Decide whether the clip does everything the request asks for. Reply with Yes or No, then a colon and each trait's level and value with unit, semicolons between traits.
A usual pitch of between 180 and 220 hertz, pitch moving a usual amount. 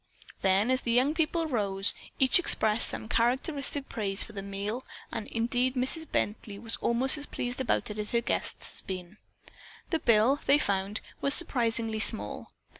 No: high, 235 Hz; average, 4.2 semitones